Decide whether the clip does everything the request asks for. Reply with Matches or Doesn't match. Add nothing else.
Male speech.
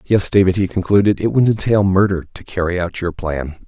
Matches